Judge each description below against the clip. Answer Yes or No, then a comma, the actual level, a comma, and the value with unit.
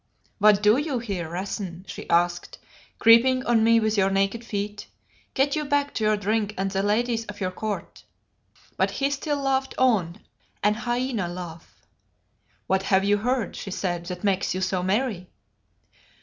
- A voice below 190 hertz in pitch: No, high, 210 Hz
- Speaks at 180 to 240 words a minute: No, average, 165 wpm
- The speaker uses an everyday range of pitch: Yes, average, 4.1 semitones